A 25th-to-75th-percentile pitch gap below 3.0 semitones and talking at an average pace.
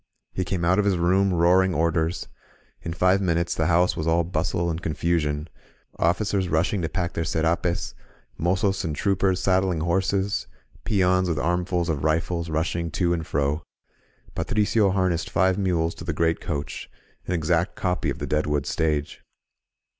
Yes: narrow, 2.4 semitones; average, 170 wpm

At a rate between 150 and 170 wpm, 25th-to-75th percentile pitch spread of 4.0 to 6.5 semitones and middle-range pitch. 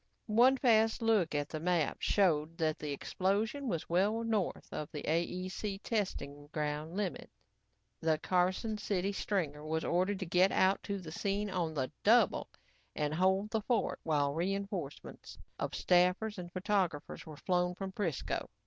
Yes: average, 155 wpm; average, 4.3 semitones; medium, 180 Hz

